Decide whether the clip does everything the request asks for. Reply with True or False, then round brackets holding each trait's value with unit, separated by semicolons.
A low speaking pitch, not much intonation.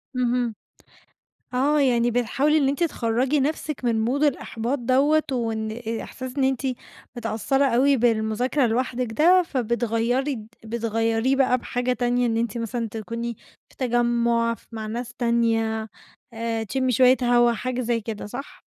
False (240 Hz; 2.3 semitones)